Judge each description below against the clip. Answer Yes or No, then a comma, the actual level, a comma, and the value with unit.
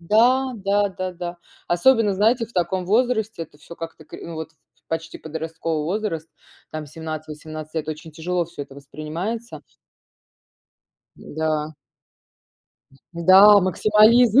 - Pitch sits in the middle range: Yes, medium, 170 Hz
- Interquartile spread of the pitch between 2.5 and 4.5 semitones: No, average, 5.1 semitones